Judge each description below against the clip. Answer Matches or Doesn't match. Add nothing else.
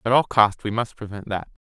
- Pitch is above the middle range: Doesn't match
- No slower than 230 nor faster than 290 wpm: Matches